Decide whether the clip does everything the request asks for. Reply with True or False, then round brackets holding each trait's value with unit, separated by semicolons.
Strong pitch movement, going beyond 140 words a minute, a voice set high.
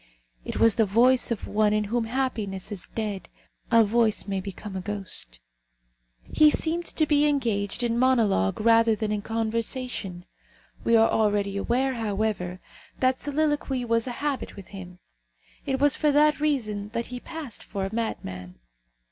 False (4.2 semitones; 160 wpm; 225 Hz)